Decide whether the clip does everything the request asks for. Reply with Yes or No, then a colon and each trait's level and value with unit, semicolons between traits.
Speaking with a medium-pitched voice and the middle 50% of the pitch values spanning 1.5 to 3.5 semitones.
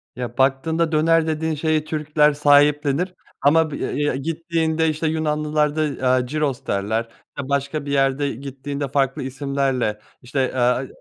Yes: medium, 145 Hz; narrow, 2.6 semitones